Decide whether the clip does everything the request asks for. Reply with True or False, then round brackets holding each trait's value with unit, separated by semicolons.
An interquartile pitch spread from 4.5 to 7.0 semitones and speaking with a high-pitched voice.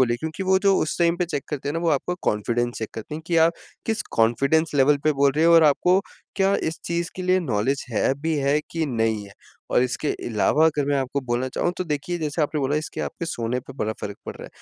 False (4.9 semitones; 145 Hz)